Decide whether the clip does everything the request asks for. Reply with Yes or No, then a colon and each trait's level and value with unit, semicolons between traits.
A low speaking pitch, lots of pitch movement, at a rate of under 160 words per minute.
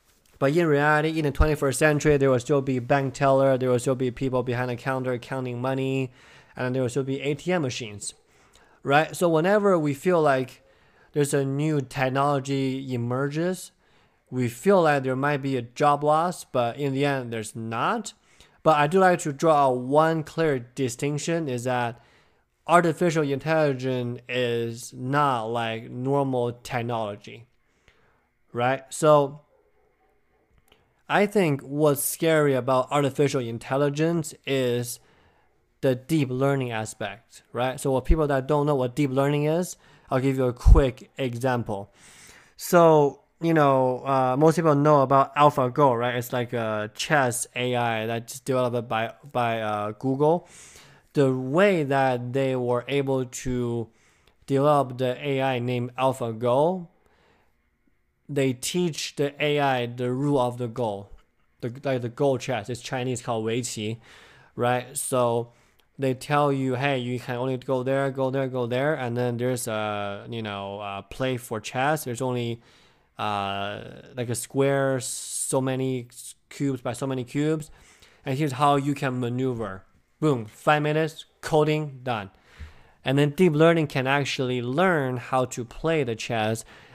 No: low, 130 Hz; average, 3.1 semitones; average, 150 wpm